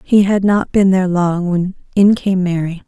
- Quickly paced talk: Yes, fast, 210 wpm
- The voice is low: No, medium, 185 Hz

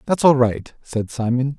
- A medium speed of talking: Yes, average, 190 wpm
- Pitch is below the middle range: Yes, low, 130 Hz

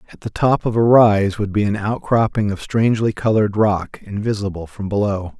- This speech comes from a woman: No, male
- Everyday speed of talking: Yes, average, 190 wpm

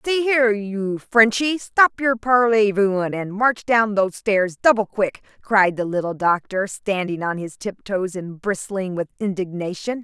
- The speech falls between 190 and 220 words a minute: No, average, 160 wpm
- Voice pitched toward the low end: No, high, 205 Hz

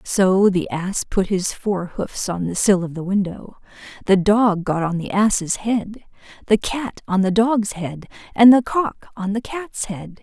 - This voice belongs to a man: No, female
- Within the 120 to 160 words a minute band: No, average, 195 wpm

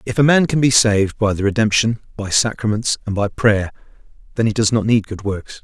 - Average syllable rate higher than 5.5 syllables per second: Yes, 5.7 syllables/s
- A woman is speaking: No, male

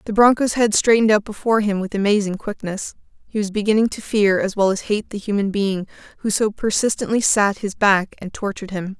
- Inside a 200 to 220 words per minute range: Yes, fast, 205 wpm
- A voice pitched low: No, high, 205 Hz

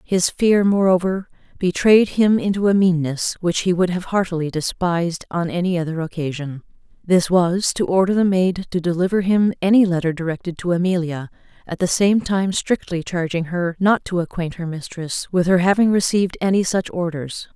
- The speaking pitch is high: No, medium, 180 Hz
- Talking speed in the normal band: Yes, average, 175 wpm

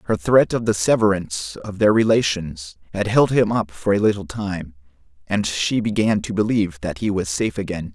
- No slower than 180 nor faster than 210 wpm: Yes, average, 195 wpm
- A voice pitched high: No, low, 100 Hz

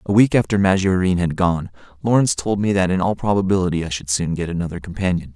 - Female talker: No, male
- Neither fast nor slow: No, fast, 215 wpm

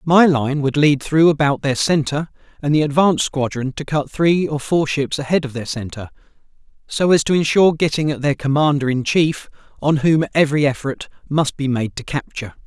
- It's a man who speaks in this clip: Yes, male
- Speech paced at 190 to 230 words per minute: Yes, average, 195 wpm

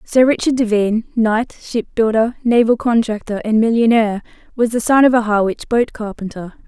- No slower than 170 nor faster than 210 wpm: No, average, 155 wpm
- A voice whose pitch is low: No, high, 225 Hz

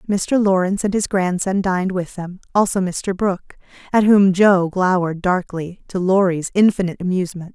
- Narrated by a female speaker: Yes, female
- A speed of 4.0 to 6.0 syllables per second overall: Yes, 5.3 syllables/s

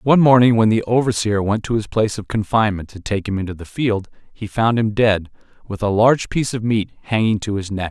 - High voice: No, low, 110 Hz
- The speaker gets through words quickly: Yes, fast, 235 wpm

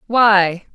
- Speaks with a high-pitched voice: Yes, high, 205 Hz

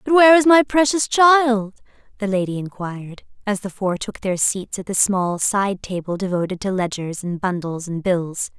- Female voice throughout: Yes, female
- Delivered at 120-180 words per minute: No, average, 190 wpm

